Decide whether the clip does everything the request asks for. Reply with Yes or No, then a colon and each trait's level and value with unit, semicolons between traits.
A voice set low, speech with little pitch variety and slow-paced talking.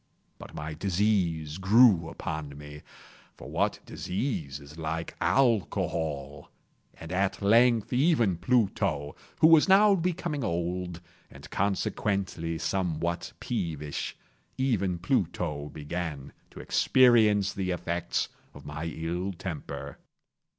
No: very low, 90 Hz; wide, 5.5 semitones; slow, 100 wpm